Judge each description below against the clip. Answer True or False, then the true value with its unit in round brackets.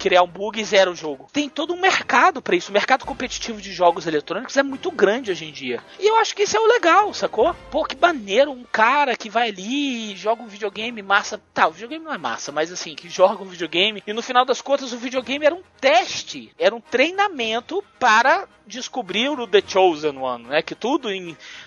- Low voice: False (230 Hz)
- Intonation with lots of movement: True (6.8 semitones)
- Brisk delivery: True (225 wpm)